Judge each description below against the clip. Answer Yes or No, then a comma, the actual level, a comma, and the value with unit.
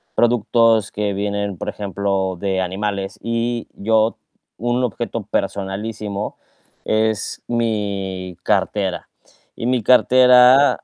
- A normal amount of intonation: Yes, average, 3.0 semitones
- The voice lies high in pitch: No, low, 105 Hz